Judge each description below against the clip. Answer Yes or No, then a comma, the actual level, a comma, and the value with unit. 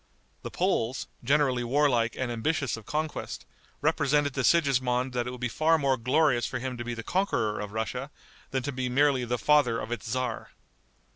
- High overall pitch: No, low, 130 Hz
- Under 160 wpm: No, average, 190 wpm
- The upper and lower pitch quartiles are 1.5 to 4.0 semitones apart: Yes, average, 3.4 semitones